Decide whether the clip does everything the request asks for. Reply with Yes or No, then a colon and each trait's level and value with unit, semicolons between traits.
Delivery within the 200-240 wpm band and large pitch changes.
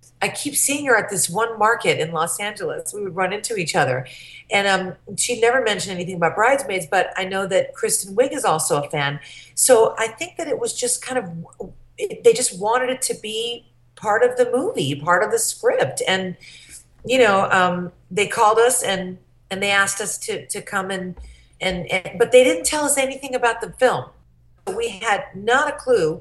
Yes: fast, 205 wpm; wide, 5.8 semitones